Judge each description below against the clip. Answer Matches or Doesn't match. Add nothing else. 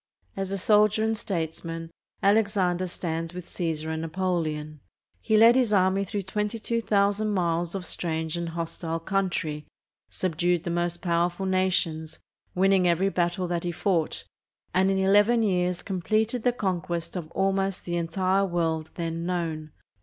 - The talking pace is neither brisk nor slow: Matches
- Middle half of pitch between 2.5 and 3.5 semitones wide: Matches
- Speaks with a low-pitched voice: Doesn't match